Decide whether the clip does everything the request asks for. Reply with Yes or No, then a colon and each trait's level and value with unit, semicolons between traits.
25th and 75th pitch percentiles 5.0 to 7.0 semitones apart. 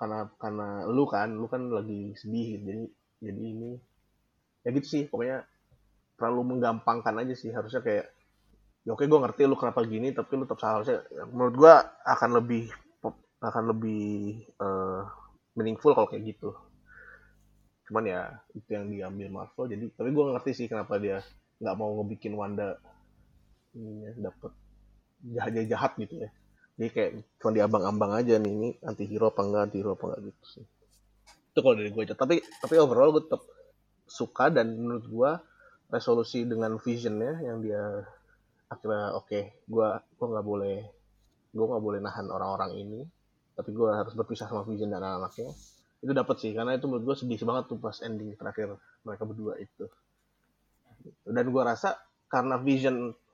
No: average, 2.9 semitones